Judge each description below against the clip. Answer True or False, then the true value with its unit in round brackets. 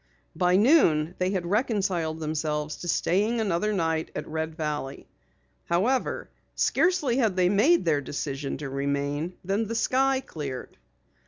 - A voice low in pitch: False (175 Hz)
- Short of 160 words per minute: True (140 wpm)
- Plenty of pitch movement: True (6.2 semitones)